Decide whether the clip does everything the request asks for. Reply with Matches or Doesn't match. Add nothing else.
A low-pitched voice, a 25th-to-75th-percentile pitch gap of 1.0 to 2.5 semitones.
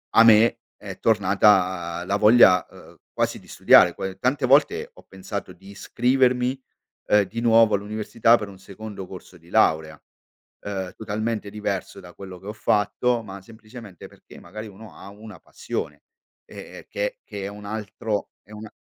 Doesn't match